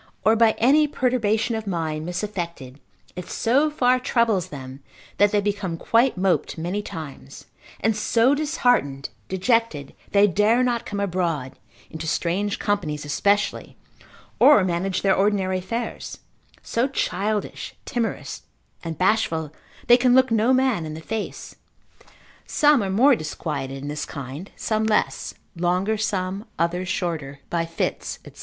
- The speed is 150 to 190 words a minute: No, average, 140 wpm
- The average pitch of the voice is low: No, high, 200 Hz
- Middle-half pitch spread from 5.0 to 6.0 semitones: Yes, wide, 5.5 semitones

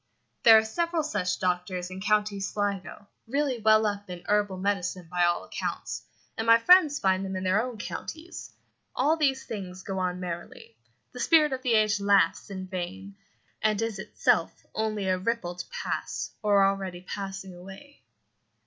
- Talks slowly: No, average, 165 wpm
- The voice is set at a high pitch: Yes, high, 200 Hz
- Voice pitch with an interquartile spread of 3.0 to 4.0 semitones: Yes, average, 3.6 semitones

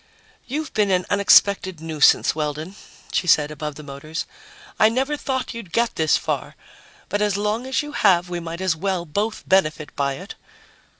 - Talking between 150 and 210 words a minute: Yes, average, 175 wpm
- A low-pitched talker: No, medium, 185 Hz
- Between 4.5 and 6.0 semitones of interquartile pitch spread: Yes, wide, 5.5 semitones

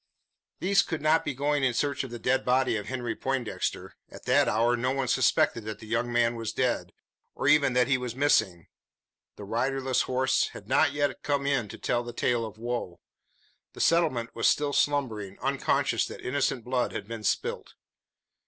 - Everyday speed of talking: Yes, average, 190 wpm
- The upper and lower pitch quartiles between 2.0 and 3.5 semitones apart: Yes, average, 3.0 semitones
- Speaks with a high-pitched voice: No, low, 125 Hz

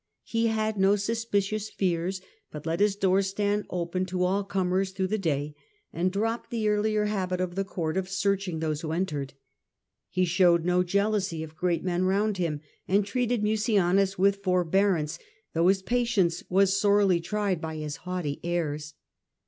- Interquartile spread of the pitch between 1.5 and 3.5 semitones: Yes, average, 2.8 semitones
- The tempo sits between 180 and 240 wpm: No, average, 165 wpm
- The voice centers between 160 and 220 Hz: Yes, high, 190 Hz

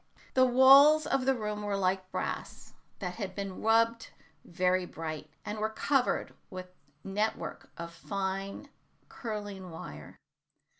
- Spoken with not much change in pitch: No, average, 3.7 semitones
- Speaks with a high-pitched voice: Yes, high, 200 Hz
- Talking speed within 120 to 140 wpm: Yes, slow, 135 wpm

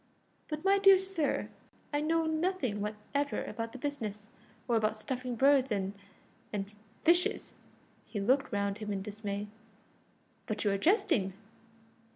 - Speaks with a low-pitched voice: No, high, 235 Hz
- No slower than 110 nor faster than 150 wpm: Yes, average, 140 wpm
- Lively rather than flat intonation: Yes, wide, 6.7 semitones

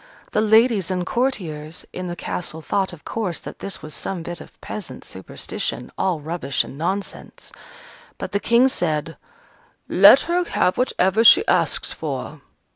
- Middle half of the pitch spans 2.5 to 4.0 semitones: No, average, 5.1 semitones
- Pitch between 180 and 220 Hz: Yes, medium, 185 Hz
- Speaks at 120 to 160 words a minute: Yes, average, 155 wpm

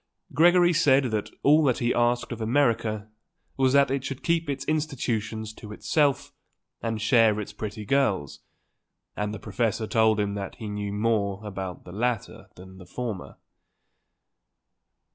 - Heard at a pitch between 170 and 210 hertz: No, low, 110 Hz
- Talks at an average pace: Yes, average, 150 wpm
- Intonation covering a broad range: No, average, 4.4 semitones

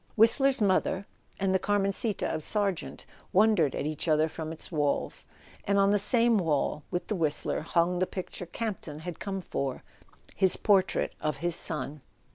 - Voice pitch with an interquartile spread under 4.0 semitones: No, average, 4.4 semitones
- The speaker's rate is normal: Yes, average, 170 wpm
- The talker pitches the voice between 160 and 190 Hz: Yes, medium, 185 Hz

